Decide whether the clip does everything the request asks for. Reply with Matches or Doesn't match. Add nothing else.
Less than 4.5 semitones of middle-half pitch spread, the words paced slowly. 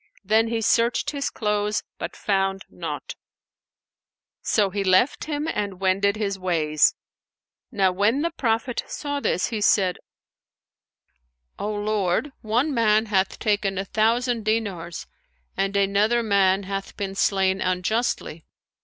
Matches